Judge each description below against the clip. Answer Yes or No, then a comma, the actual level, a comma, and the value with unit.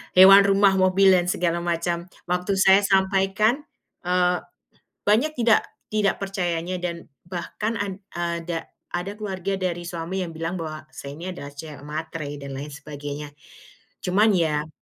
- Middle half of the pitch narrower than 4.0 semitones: Yes, average, 2.9 semitones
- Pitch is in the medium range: Yes, medium, 180 Hz